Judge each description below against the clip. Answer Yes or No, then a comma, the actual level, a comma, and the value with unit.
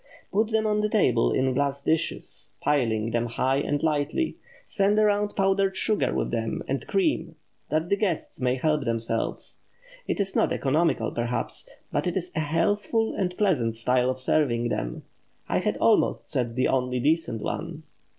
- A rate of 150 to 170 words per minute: Yes, average, 165 wpm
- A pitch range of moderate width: No, wide, 7.6 semitones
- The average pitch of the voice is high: No, medium, 150 Hz